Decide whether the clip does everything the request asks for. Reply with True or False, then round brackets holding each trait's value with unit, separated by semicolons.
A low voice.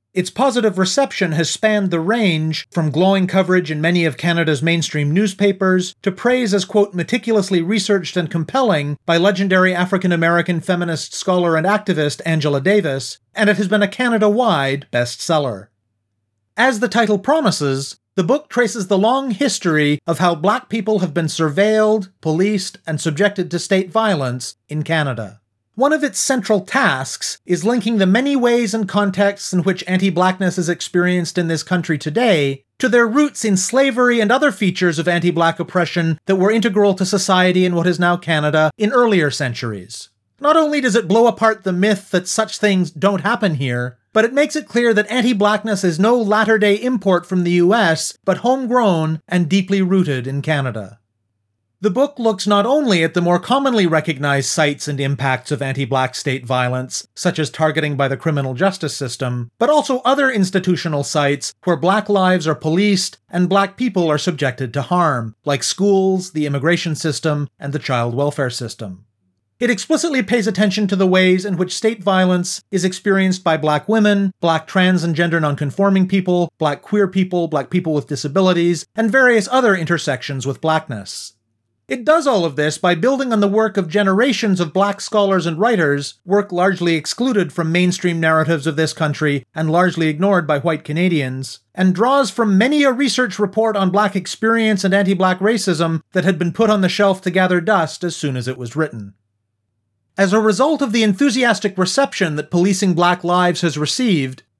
False (180 Hz)